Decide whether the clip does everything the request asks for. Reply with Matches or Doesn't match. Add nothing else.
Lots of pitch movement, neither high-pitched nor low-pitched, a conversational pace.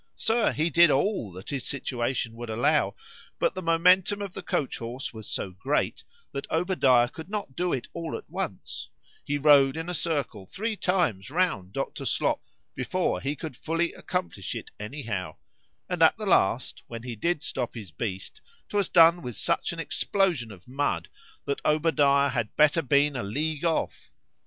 Matches